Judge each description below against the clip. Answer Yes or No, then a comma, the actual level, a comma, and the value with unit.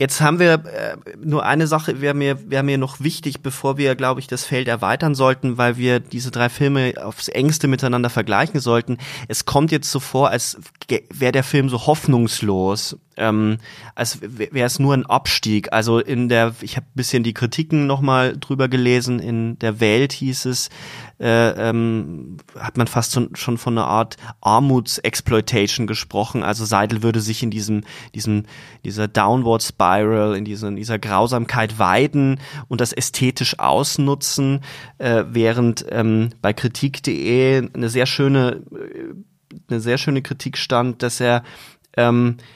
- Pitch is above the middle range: No, low, 125 Hz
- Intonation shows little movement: No, average, 3.3 semitones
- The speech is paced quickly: No, average, 160 wpm